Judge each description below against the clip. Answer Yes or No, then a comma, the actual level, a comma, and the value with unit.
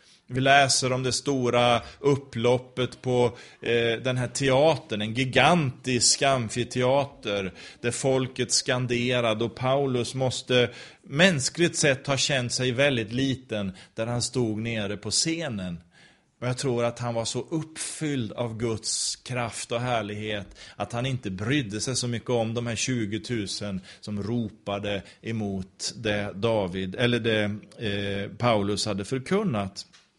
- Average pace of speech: Yes, average, 135 wpm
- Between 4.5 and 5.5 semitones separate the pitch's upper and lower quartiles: No, average, 3.4 semitones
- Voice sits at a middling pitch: No, low, 120 Hz